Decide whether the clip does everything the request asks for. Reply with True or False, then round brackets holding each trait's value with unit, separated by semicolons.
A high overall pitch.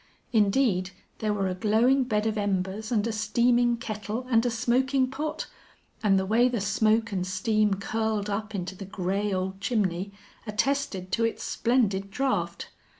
True (215 Hz)